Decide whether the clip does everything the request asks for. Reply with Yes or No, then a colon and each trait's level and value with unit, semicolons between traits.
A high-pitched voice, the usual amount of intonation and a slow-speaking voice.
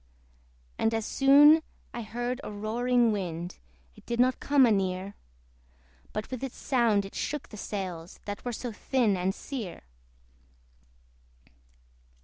Yes: high, 225 Hz; average, 4.1 semitones; slow, 130 wpm